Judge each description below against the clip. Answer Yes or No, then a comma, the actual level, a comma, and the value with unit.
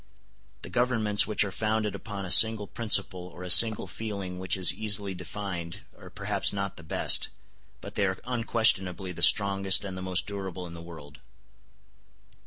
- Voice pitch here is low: Yes, low, 100 Hz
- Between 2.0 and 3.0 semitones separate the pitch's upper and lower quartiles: Yes, average, 2.7 semitones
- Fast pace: No, average, 170 wpm